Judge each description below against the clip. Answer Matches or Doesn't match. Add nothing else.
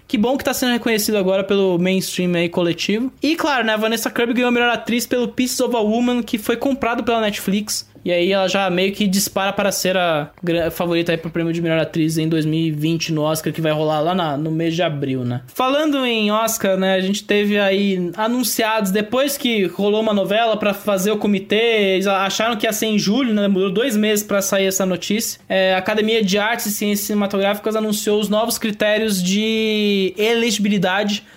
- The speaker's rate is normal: Doesn't match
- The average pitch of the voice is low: Doesn't match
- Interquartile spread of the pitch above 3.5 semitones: Doesn't match